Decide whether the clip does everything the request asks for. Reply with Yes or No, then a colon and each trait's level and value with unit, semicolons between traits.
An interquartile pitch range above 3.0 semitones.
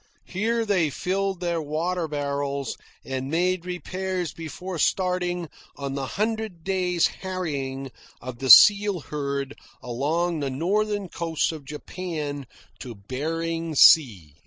Yes: average, 4.6 semitones